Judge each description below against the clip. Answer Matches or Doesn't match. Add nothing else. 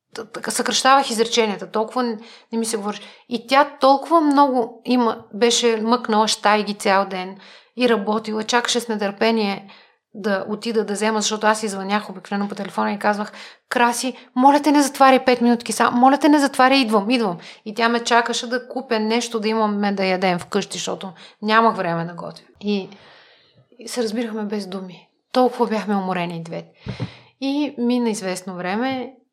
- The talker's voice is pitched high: Matches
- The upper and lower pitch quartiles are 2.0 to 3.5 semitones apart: Matches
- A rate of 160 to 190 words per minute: Matches